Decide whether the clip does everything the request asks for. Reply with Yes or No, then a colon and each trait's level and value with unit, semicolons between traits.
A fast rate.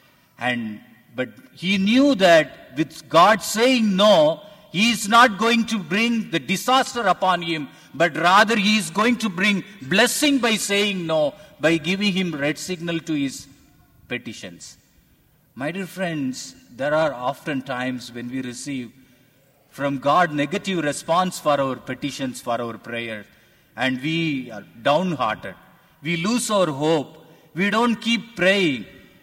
No: average, 145 wpm